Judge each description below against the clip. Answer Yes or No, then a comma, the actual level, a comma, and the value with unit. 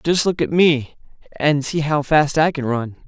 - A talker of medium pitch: Yes, medium, 150 Hz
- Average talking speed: No, fast, 215 wpm